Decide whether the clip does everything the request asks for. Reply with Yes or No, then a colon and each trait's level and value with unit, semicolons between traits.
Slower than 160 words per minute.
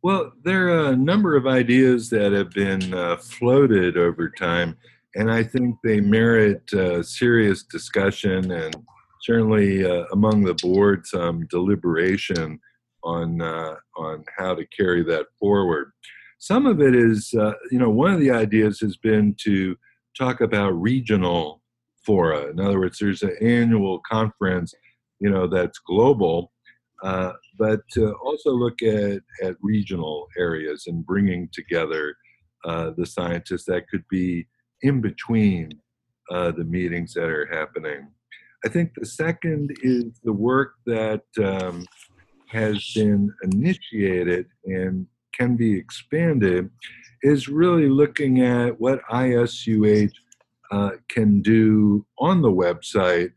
Yes: slow, 135 wpm